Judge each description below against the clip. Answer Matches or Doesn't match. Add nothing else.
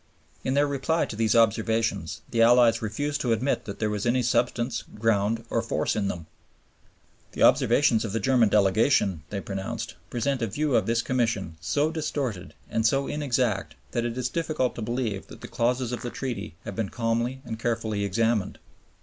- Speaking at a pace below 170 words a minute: Doesn't match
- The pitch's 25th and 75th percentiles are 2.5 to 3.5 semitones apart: Matches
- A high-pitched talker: Doesn't match